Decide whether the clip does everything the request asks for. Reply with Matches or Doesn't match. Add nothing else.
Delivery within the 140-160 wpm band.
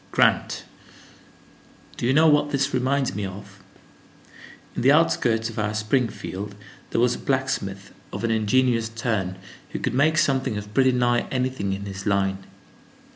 Matches